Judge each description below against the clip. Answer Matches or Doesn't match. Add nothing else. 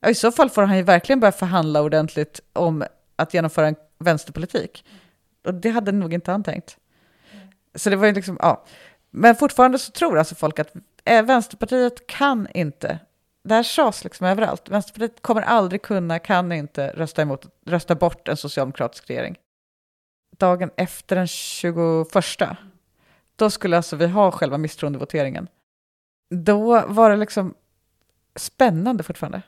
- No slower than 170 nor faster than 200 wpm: Doesn't match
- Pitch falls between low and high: Matches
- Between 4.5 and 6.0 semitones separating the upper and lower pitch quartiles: Matches